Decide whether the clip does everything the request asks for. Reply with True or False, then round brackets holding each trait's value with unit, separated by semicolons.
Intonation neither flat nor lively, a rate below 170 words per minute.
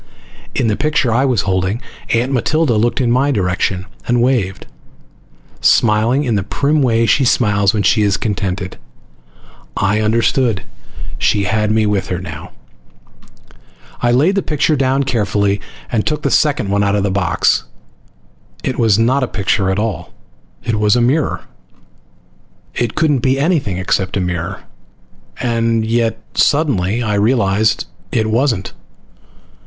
True (4.3 semitones; 150 wpm)